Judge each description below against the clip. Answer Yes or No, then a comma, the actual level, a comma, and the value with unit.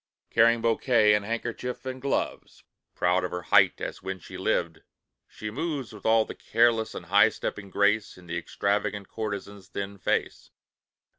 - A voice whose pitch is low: Yes, low, 105 Hz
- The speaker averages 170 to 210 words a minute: No, average, 160 wpm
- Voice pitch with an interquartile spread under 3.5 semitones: Yes, average, 2.8 semitones